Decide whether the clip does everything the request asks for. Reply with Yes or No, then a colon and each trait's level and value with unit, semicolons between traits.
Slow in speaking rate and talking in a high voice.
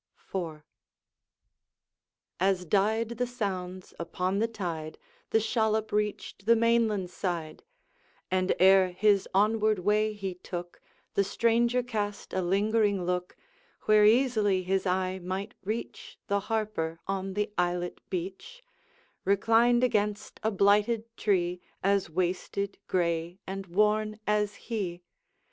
Yes: slow, 120 wpm; high, 200 Hz